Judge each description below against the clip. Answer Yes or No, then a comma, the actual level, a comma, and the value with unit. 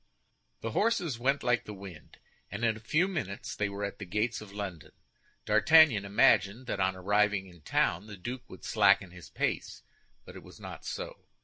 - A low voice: Yes, low, 105 Hz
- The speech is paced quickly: No, average, 190 wpm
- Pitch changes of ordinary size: Yes, average, 3.7 semitones